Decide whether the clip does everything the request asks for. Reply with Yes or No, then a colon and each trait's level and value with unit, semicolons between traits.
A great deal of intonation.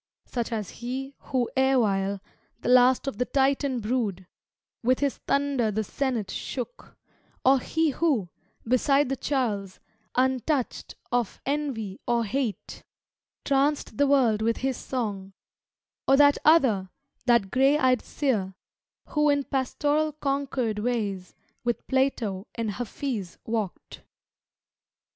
No: average, 4.1 semitones